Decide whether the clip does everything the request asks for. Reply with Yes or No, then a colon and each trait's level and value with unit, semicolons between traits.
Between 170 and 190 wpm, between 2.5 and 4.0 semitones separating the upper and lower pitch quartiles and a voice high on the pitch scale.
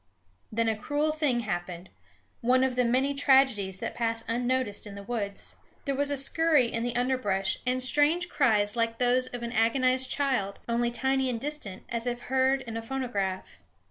Yes: average, 180 wpm; average, 2.8 semitones; high, 245 Hz